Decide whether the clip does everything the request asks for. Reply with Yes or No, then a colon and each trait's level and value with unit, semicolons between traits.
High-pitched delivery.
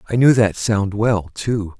No: low, 105 Hz